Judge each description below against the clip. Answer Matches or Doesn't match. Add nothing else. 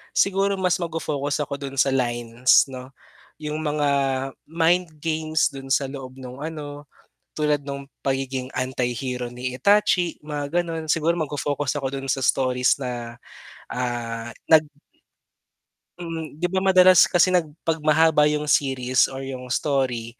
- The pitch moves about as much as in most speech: Matches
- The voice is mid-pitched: Matches